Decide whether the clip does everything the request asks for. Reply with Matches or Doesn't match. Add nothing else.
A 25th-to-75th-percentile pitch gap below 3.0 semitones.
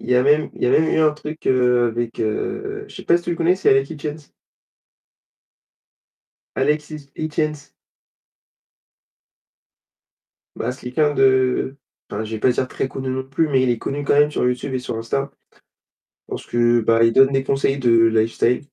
Doesn't match